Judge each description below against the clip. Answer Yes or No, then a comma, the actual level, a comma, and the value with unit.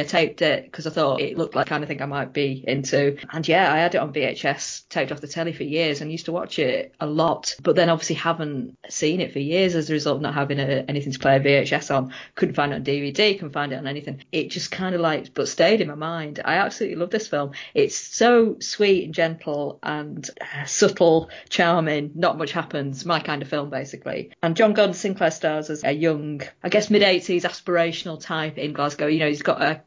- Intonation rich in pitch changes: No, average, 3.4 semitones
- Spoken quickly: Yes, fast, 245 wpm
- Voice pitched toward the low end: No, medium, 155 Hz